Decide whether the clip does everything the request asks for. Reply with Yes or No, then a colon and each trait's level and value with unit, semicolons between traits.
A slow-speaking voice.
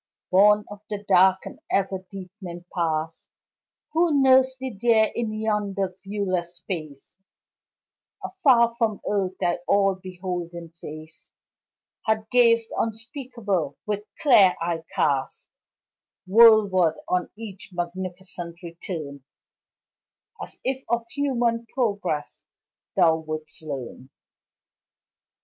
Yes: slow, 100 wpm